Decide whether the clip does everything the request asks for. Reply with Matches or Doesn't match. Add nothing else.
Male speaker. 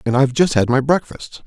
Matches